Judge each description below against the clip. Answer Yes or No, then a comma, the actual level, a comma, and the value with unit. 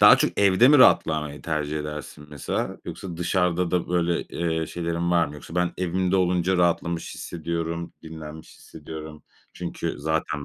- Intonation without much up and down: Yes, narrow, 2.2 semitones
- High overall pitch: No, very low, 85 Hz